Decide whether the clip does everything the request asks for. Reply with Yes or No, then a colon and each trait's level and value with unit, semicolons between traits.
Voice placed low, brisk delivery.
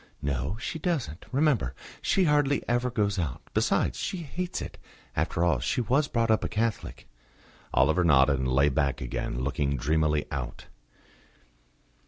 No: very low, 85 Hz; average, 150 wpm